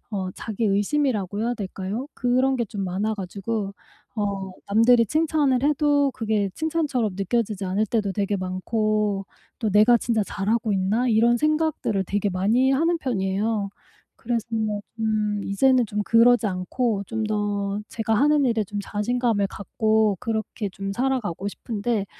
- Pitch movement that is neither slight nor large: Yes, average, 3.3 semitones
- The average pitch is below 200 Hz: No, high, 215 Hz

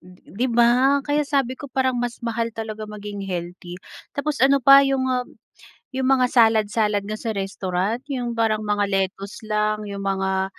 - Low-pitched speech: No, high, 220 Hz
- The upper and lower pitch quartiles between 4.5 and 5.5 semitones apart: No, average, 4.1 semitones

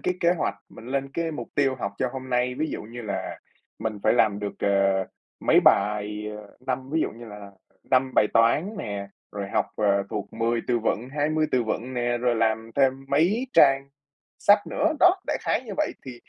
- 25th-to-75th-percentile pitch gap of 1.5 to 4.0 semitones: No, average, 4.7 semitones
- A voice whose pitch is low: Yes, low, 120 Hz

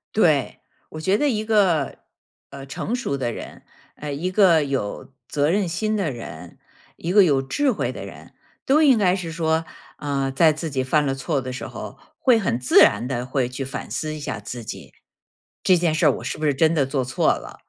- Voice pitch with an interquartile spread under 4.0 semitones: No, average, 5.3 semitones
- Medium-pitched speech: Yes, medium, 150 Hz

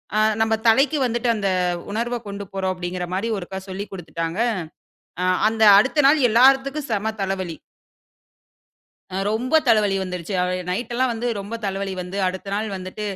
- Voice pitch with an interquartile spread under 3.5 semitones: No, average, 4.1 semitones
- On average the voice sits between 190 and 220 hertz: Yes, high, 205 Hz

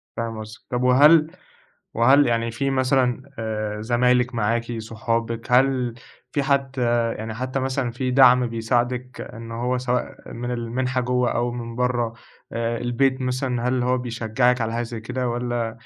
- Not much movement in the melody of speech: Yes, narrow, 1.7 semitones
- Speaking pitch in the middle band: No, low, 120 Hz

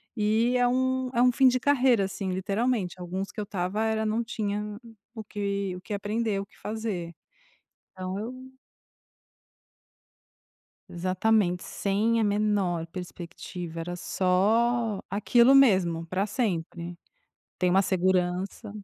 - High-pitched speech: Yes, high, 200 Hz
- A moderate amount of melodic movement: Yes, average, 3.6 semitones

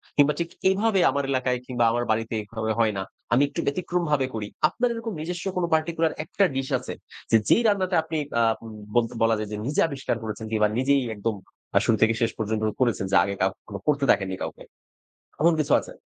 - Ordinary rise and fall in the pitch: No, wide, 6.6 semitones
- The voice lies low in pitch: Yes, low, 130 Hz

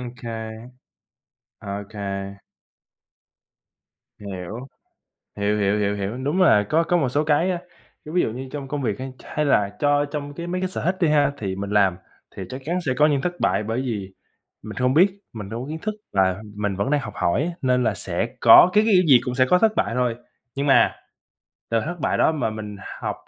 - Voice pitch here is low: Yes, low, 130 Hz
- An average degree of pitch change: No, wide, 6.7 semitones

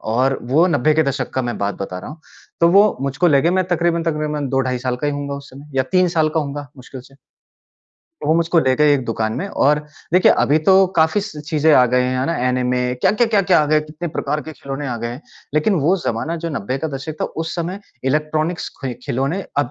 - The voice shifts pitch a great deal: No, average, 3.7 semitones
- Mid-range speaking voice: Yes, medium, 150 Hz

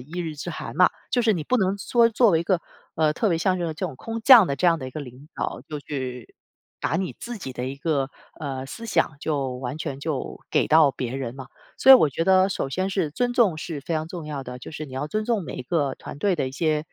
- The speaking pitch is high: No, medium, 155 Hz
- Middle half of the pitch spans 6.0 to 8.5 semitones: No, wide, 5.6 semitones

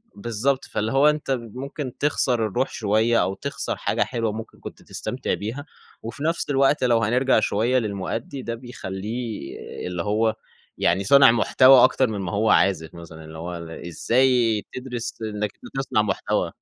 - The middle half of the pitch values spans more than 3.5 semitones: Yes, average, 3.9 semitones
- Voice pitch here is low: Yes, low, 115 Hz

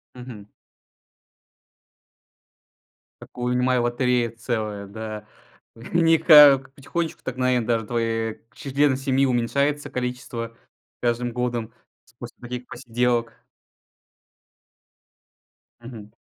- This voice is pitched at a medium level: No, low, 125 Hz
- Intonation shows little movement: Yes, narrow, 2.1 semitones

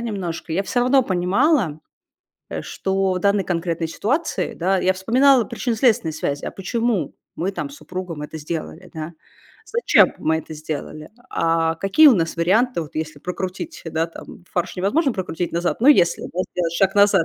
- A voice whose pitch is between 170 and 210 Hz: Yes, medium, 185 Hz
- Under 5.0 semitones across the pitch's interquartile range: No, average, 5.3 semitones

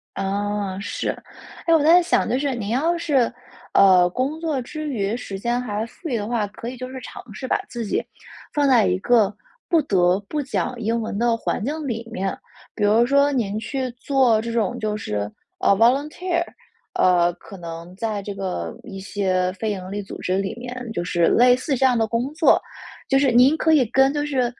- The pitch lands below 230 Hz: No, high, 235 Hz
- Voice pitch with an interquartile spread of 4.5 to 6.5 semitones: Yes, average, 5.2 semitones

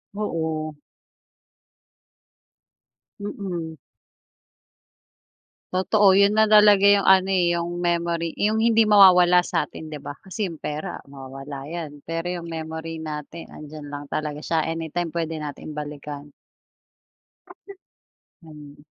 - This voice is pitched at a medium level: Yes, medium, 165 Hz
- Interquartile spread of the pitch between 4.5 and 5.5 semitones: No, average, 3.8 semitones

